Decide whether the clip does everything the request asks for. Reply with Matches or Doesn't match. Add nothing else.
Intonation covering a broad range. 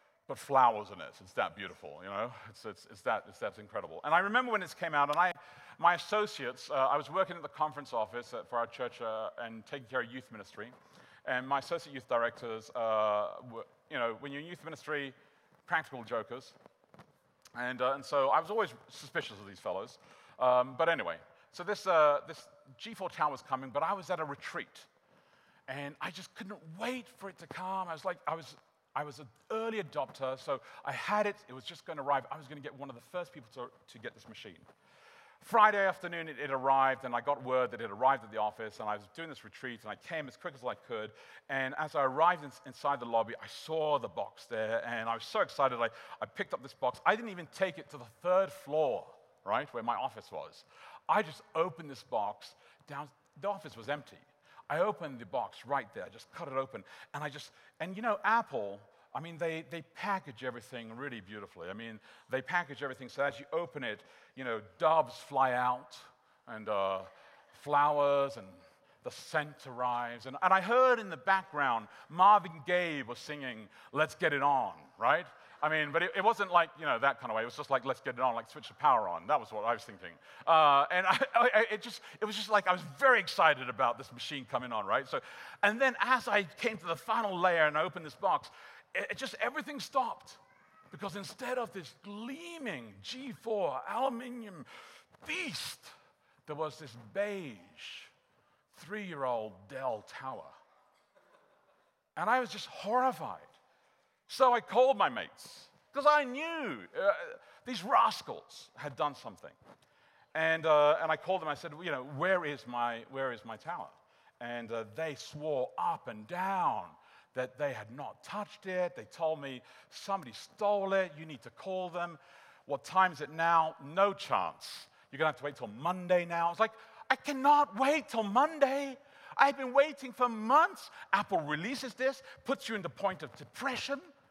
Matches